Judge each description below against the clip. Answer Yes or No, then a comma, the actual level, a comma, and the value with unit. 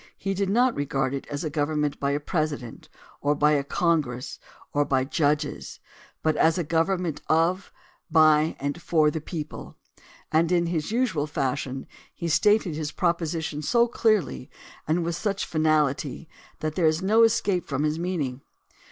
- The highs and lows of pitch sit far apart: No, average, 3.2 semitones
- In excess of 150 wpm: Yes, average, 160 wpm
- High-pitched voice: No, medium, 155 Hz